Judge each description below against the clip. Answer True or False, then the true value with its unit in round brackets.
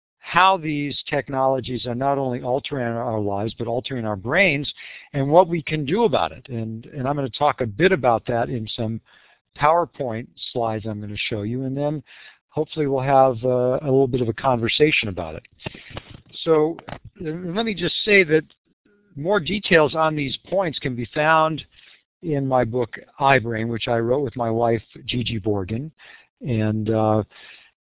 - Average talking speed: True (175 wpm)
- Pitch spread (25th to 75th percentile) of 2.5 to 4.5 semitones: False (4.9 semitones)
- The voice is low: True (130 Hz)